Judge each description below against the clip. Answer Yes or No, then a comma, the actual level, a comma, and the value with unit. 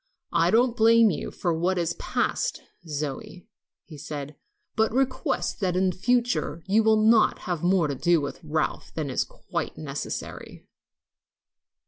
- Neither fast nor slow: Yes, average, 145 wpm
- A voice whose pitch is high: No, medium, 180 Hz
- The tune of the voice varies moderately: No, wide, 5.9 semitones